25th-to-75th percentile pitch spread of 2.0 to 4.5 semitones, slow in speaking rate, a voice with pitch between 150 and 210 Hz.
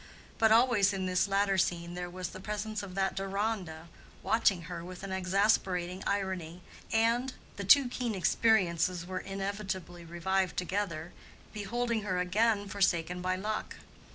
Yes: average, 2.7 semitones; slow, 130 wpm; high, 190 Hz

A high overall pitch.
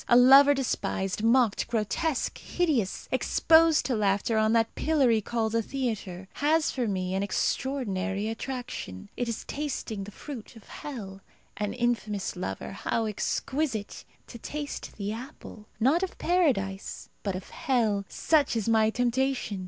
Yes: high, 230 Hz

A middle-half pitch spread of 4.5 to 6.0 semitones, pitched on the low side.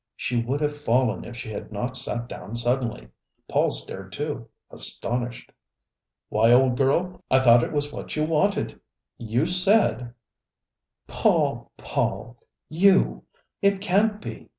Yes: average, 4.9 semitones; low, 130 Hz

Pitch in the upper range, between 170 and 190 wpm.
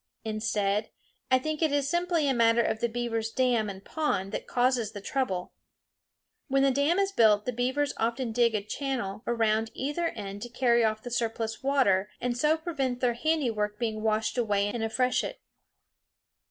Yes: high, 235 Hz; average, 180 wpm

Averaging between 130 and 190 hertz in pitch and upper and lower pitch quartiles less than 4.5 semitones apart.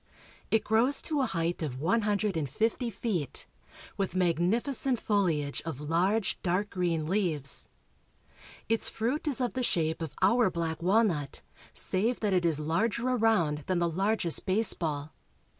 No: medium, 185 Hz; wide, 5.5 semitones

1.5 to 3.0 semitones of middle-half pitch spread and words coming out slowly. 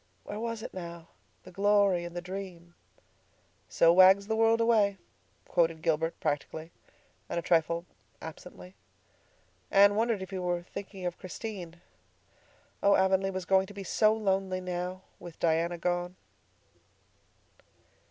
Yes: narrow, 2.6 semitones; slow, 130 wpm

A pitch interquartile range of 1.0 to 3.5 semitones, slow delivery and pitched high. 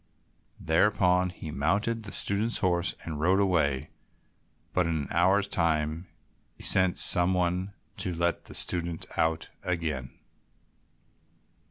No: narrow, 2.5 semitones; slow, 120 wpm; very low, 90 Hz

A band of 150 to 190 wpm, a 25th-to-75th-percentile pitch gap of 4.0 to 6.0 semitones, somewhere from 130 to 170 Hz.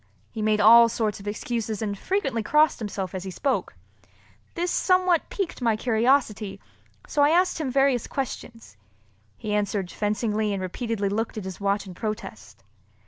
No: average, 160 wpm; average, 4.3 semitones; high, 220 Hz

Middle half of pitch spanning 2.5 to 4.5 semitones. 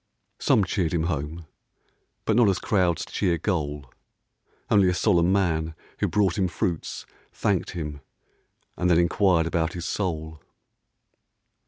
Yes: average, 2.9 semitones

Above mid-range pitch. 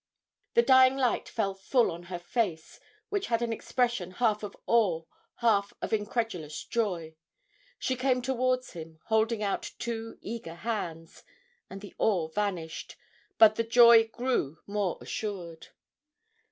Yes: high, 215 Hz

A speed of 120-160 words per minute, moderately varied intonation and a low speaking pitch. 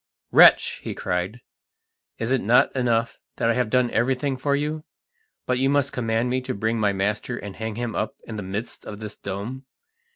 No: average, 195 wpm; average, 3.2 semitones; low, 115 Hz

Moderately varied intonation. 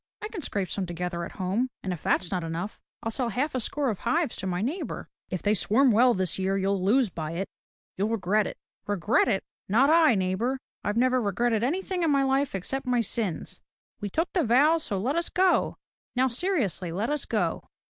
No: wide, 6.0 semitones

